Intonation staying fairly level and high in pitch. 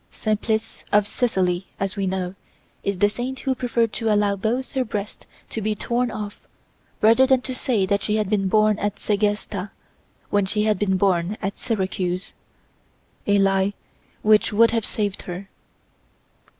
Yes: narrow, 2.3 semitones; high, 210 Hz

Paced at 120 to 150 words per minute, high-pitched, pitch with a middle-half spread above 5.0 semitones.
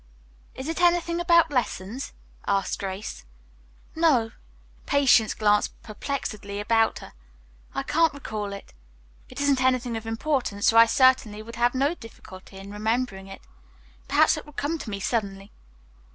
Yes: average, 145 wpm; high, 230 Hz; wide, 5.4 semitones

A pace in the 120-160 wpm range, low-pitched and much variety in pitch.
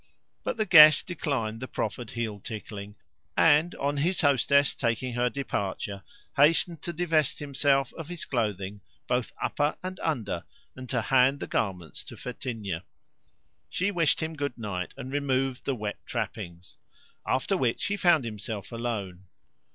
Yes: average, 150 wpm; low, 130 Hz; wide, 5.9 semitones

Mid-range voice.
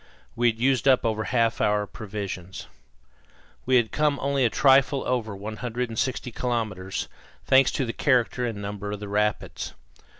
No: low, 115 Hz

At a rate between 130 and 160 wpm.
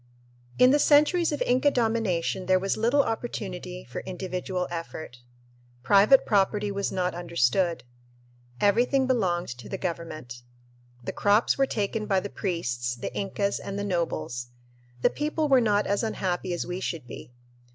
Yes: average, 150 wpm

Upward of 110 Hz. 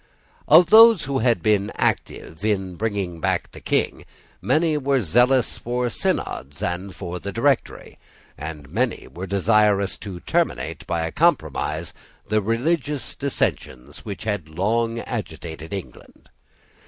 No: low, 100 Hz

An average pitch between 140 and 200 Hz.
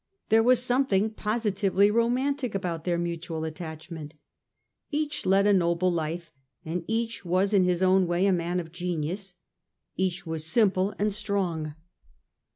Yes: medium, 185 Hz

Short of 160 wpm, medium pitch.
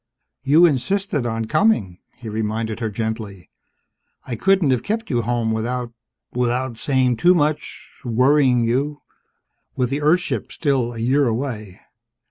No: average, 140 wpm; low, 125 Hz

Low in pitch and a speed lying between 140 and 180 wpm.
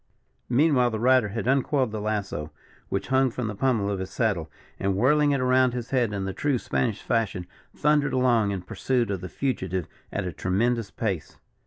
No: low, 115 Hz; average, 190 wpm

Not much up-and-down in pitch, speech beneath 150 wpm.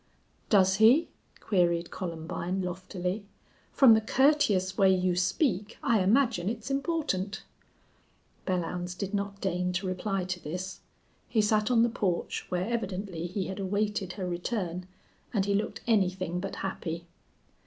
No: average, 3.0 semitones; average, 140 wpm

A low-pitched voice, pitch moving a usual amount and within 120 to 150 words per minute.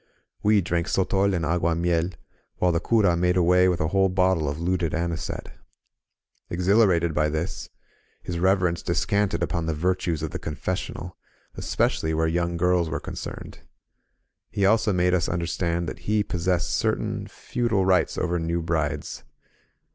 No: very low, 90 Hz; narrow, 1.9 semitones; average, 145 wpm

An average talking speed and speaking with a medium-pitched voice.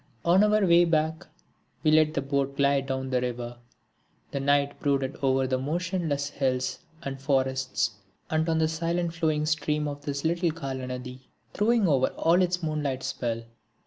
Yes: average, 160 wpm; medium, 145 Hz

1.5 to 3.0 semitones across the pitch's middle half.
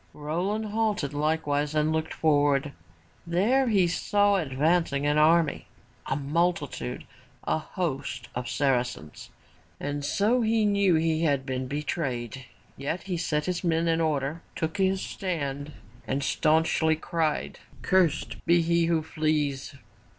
No: average, 3.5 semitones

